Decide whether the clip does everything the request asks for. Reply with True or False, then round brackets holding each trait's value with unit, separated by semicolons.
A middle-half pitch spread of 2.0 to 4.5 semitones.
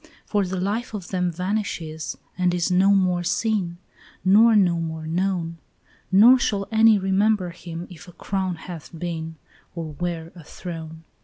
True (2.9 semitones)